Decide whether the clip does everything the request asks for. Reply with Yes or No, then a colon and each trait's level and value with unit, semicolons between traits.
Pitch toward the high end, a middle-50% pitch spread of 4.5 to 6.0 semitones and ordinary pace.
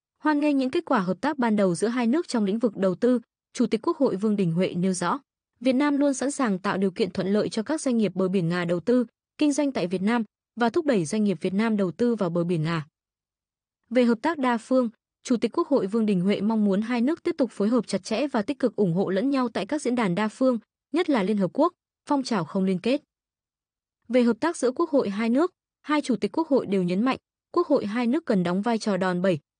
No: high, 230 Hz; average, 5.2 semitones; fast, 270 wpm